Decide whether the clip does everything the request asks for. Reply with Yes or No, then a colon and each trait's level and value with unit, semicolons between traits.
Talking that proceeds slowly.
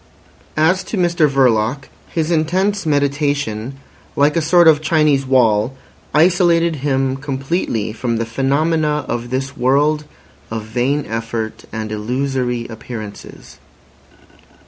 Yes: slow, 115 wpm